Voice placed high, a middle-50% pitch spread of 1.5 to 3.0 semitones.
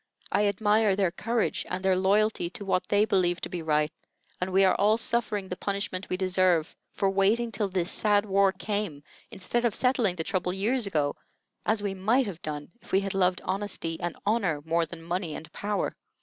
Yes: high, 195 Hz; narrow, 2.5 semitones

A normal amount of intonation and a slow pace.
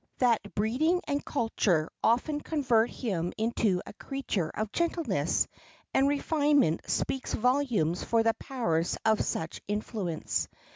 No: wide, 5.8 semitones; slow, 125 wpm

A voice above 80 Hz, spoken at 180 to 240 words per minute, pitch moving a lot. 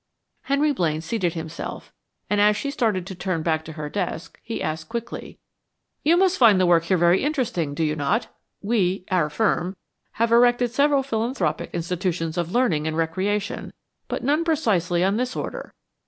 No: high, 190 Hz; average, 170 wpm; wide, 6.3 semitones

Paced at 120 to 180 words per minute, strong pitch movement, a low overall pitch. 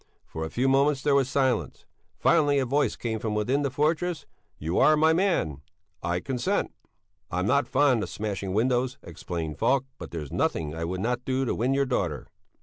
No: average, 190 wpm; wide, 7.1 semitones; low, 125 Hz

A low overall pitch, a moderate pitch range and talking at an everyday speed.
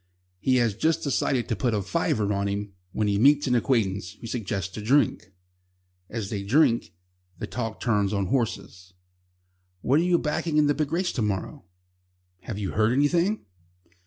No: low, 115 Hz; wide, 5.9 semitones; average, 175 wpm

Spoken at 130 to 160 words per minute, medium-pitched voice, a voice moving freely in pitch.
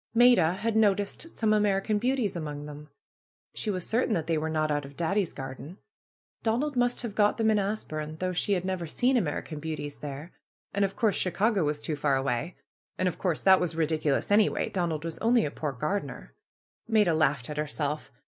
No: average, 200 wpm; medium, 175 Hz; wide, 5.7 semitones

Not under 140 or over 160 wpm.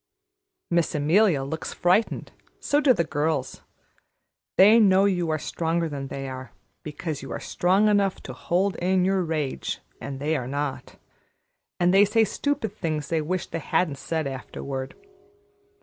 Yes: average, 155 wpm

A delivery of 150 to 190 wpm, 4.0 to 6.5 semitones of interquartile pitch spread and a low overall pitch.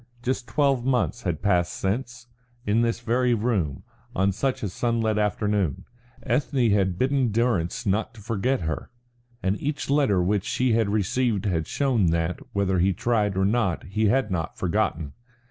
Yes: average, 170 wpm; average, 4.3 semitones; low, 105 Hz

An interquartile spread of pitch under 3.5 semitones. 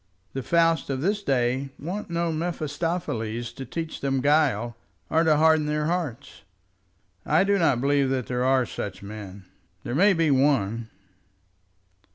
No: average, 4.9 semitones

